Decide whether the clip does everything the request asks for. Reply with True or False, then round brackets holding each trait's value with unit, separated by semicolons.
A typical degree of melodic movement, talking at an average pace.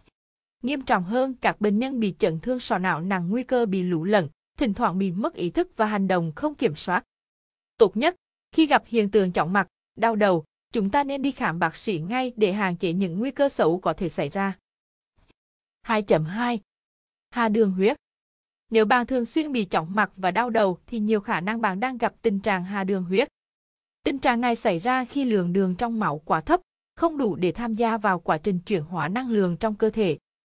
True (4.4 semitones; 220 wpm)